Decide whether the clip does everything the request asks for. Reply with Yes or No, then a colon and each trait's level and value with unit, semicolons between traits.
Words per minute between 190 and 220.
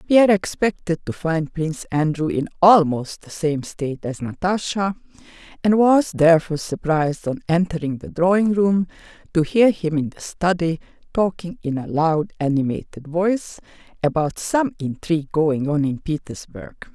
No: average, 145 wpm